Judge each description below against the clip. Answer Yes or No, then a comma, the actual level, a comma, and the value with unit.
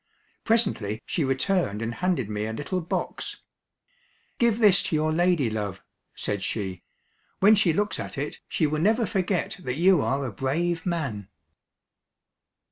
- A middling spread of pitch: No, wide, 8.5 semitones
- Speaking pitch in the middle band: Yes, medium, 155 Hz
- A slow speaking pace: No, average, 145 wpm